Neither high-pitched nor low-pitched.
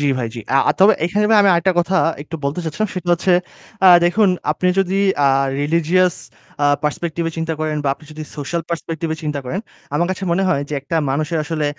Yes: medium, 165 Hz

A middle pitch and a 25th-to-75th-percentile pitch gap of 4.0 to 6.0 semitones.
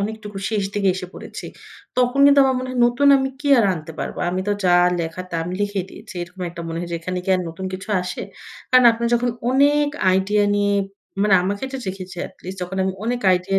No: high, 200 Hz; average, 5.0 semitones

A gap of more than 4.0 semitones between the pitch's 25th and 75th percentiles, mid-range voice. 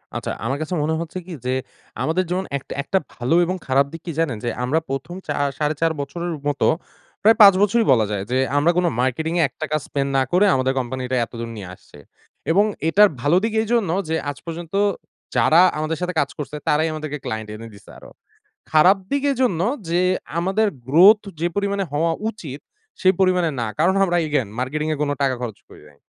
Yes: wide, 5.4 semitones; medium, 160 Hz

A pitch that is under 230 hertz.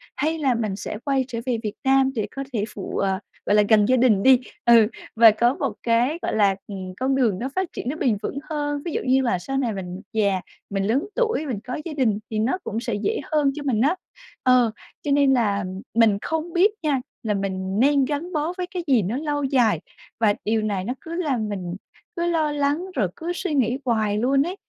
No: very high, 250 Hz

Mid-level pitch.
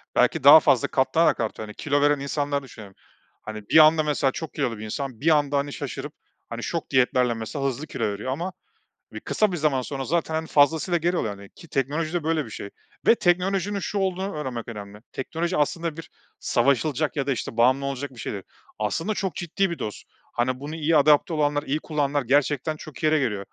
Yes: medium, 145 Hz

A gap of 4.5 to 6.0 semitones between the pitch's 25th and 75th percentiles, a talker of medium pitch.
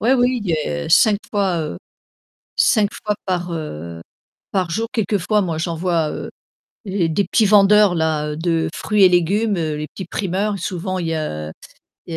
No: average, 4.1 semitones; medium, 180 Hz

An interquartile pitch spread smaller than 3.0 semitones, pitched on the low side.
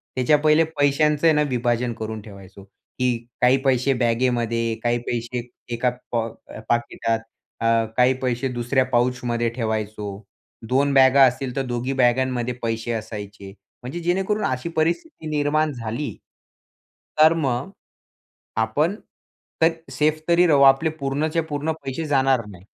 No: average, 3.8 semitones; low, 125 Hz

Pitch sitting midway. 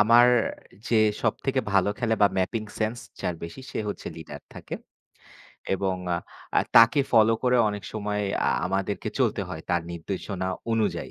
No: low, 105 Hz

